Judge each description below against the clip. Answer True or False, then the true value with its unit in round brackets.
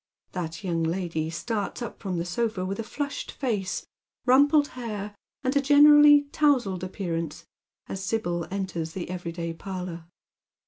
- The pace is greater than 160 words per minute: False (140 wpm)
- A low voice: False (190 Hz)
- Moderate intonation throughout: False (6.3 semitones)